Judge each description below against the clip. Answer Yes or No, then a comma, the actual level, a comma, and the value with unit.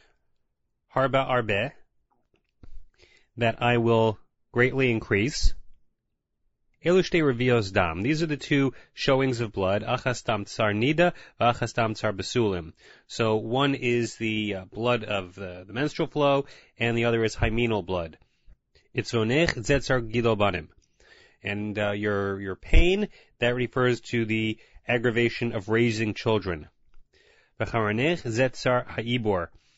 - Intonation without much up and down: No, average, 3.2 semitones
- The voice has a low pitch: Yes, low, 115 Hz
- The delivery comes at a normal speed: No, slow, 85 wpm